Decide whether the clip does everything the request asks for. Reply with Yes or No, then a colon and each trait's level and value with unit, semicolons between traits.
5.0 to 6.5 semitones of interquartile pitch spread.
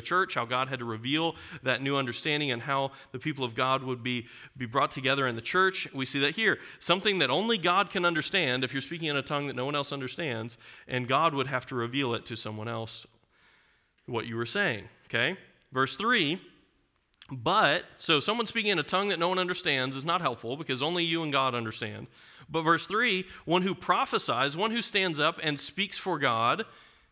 Yes: average, 5.3 semitones